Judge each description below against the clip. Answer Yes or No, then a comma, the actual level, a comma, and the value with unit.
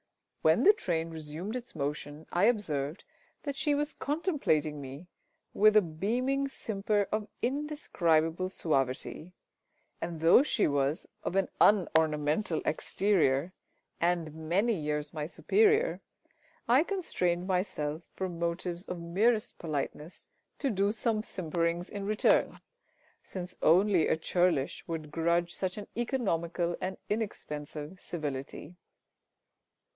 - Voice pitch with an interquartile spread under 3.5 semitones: No, average, 5.3 semitones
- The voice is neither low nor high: Yes, medium, 175 Hz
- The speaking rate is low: Yes, slow, 120 wpm